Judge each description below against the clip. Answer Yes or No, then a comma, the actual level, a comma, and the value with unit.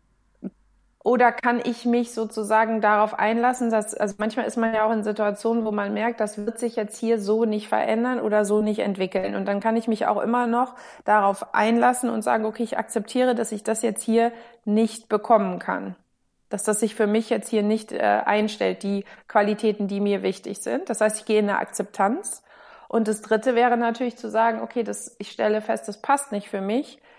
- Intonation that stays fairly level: Yes, narrow, 2.0 semitones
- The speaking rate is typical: No, fast, 205 wpm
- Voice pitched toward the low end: No, high, 220 Hz